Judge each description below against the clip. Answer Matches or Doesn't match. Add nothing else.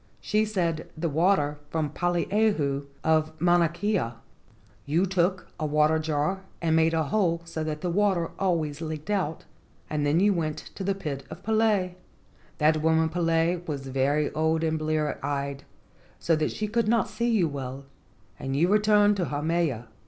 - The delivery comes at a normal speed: Matches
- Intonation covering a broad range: Doesn't match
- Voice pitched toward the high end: Doesn't match